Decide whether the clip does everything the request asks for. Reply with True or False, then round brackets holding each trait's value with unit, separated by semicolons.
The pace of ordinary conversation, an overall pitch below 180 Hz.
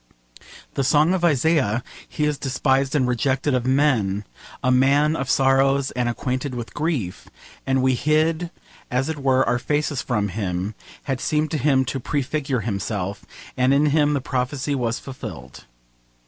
True (160 wpm; 135 Hz)